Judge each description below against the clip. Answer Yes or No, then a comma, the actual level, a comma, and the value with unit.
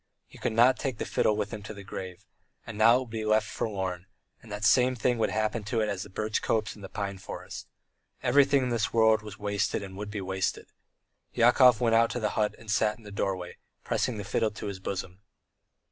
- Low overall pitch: Yes, low, 110 Hz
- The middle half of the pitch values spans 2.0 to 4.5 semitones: Yes, narrow, 2.4 semitones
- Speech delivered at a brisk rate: Yes, fast, 235 wpm